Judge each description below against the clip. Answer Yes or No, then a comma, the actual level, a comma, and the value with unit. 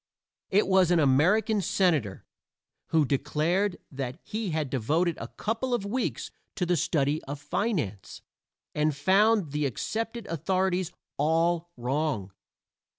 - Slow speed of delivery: Yes, slow, 125 wpm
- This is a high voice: No, medium, 165 Hz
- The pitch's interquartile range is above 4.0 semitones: Yes, wide, 5.4 semitones